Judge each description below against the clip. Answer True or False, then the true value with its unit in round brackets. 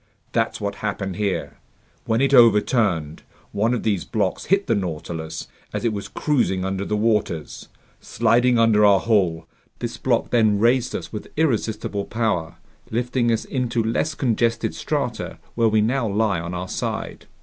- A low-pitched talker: True (110 Hz)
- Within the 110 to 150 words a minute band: False (160 wpm)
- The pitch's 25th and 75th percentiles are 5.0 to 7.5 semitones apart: False (3.4 semitones)